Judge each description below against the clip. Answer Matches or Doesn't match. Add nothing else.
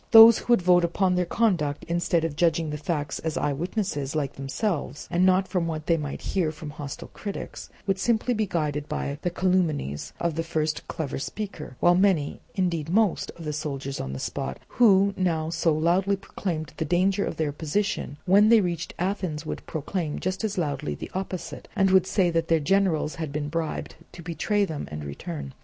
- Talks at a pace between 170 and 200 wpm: Matches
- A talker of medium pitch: Matches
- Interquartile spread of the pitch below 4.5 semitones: Matches